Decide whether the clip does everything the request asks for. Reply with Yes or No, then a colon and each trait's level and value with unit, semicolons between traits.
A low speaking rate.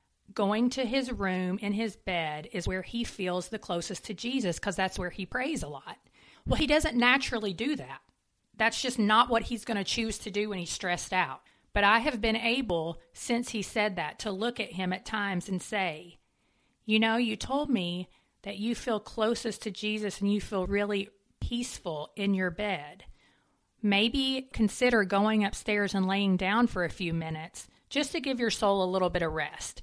No: average, 200 wpm